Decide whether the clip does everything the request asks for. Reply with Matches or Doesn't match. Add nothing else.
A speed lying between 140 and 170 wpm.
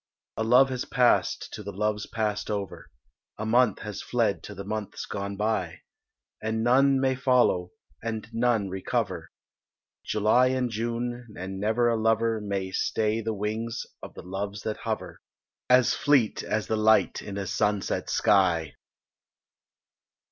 Matches